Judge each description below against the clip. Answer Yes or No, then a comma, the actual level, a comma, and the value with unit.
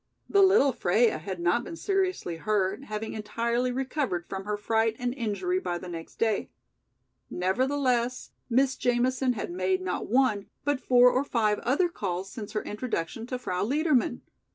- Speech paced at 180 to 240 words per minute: No, average, 160 wpm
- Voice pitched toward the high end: Yes, high, 235 Hz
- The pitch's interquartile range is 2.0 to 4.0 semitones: No, average, 4.7 semitones